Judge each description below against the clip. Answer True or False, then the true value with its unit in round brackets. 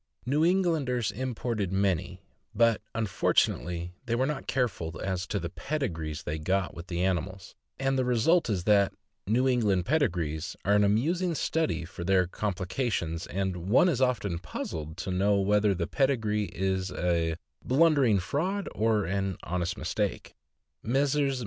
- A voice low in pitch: True (100 Hz)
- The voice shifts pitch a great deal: True (6.3 semitones)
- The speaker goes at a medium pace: True (150 wpm)